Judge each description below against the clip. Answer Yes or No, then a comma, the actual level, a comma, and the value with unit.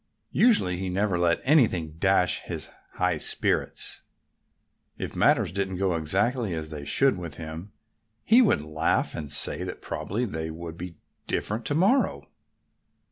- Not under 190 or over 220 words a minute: No, average, 145 wpm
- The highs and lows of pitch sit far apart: Yes, wide, 5.7 semitones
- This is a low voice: Yes, very low, 90 Hz